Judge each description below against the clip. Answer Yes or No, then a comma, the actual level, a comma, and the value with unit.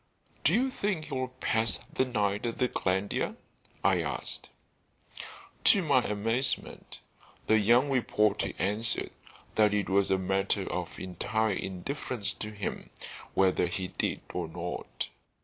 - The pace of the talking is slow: Yes, slow, 130 wpm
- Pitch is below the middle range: Yes, low, 105 Hz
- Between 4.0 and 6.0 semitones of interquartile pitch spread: Yes, average, 4.7 semitones